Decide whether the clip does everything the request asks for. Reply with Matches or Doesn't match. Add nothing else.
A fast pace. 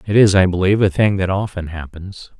Matches